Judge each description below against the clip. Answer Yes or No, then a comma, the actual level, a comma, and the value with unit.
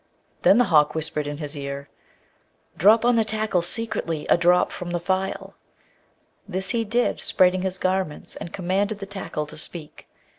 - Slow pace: No, average, 170 wpm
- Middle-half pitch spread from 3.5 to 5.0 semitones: Yes, average, 4.3 semitones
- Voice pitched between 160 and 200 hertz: Yes, medium, 185 Hz